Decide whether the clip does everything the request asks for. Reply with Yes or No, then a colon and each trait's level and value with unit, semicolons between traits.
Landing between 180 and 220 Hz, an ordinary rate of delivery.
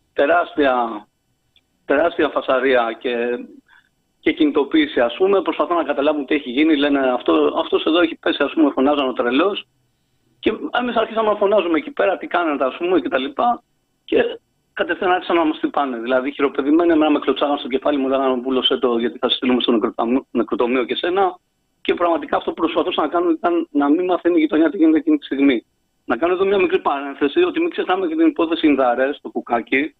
No: medium, 185 Hz; fast, 195 wpm